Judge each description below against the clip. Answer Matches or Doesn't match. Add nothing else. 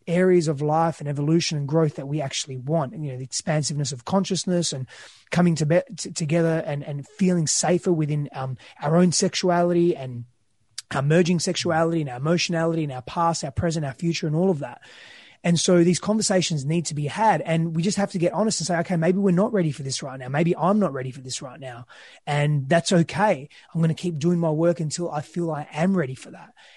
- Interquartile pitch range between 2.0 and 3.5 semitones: Matches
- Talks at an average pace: Doesn't match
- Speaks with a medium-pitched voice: Matches